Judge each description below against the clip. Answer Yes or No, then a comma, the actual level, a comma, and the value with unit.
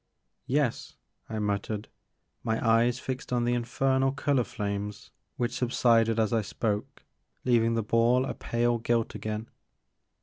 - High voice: No, low, 115 Hz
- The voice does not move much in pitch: Yes, narrow, 2.0 semitones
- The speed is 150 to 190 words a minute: No, average, 140 wpm